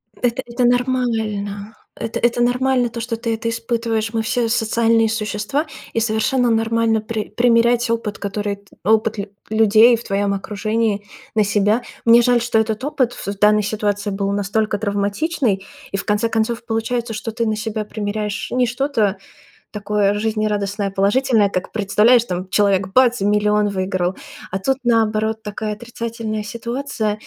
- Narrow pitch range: Yes, narrow, 2.1 semitones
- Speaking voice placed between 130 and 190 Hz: No, high, 220 Hz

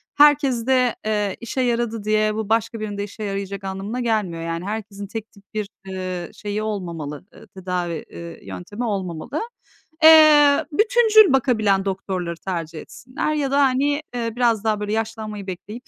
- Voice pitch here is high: Yes, high, 215 Hz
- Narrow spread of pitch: No, average, 4.3 semitones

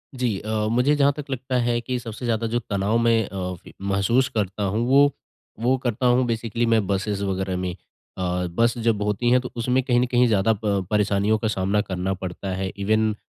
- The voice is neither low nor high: No, low, 110 Hz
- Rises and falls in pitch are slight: No, average, 3.6 semitones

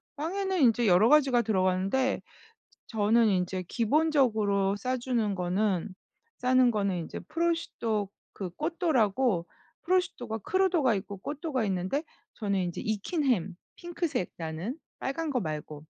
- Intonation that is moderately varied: No, wide, 6.8 semitones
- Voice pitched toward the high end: Yes, high, 225 Hz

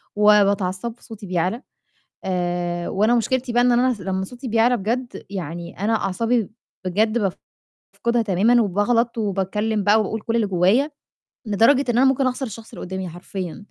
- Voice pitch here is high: Yes, high, 215 Hz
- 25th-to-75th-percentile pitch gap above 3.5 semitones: Yes, average, 4.0 semitones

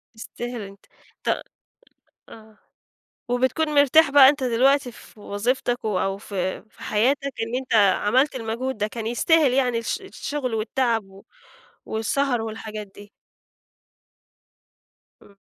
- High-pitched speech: Yes, high, 235 Hz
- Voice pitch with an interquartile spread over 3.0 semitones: Yes, average, 3.5 semitones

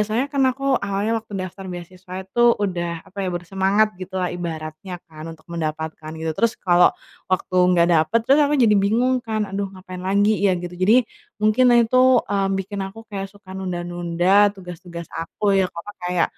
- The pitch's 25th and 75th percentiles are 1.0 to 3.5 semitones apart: Yes, average, 3.1 semitones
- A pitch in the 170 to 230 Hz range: Yes, high, 190 Hz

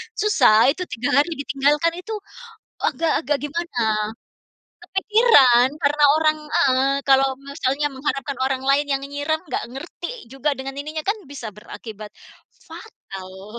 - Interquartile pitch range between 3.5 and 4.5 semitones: No, average, 3.1 semitones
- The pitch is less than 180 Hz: No, very high, 280 Hz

